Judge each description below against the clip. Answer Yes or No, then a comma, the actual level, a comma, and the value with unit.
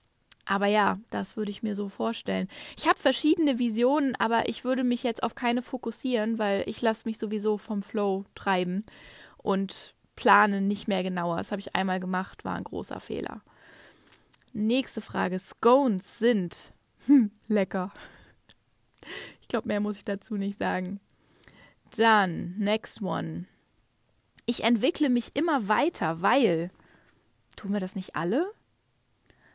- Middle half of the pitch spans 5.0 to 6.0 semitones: No, average, 4.2 semitones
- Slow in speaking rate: No, average, 140 wpm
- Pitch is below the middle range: No, high, 205 Hz